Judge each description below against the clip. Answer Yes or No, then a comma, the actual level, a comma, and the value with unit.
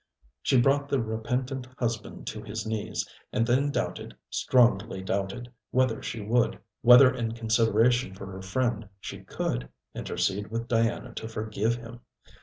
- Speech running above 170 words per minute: No, average, 145 wpm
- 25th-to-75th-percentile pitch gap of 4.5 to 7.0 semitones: No, narrow, 2.4 semitones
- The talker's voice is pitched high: No, low, 115 Hz